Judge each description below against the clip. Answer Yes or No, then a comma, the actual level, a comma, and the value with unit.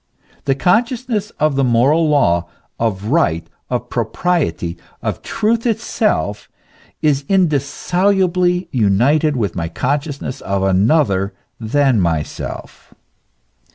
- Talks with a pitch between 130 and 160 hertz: Yes, medium, 140 Hz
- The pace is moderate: No, slow, 100 wpm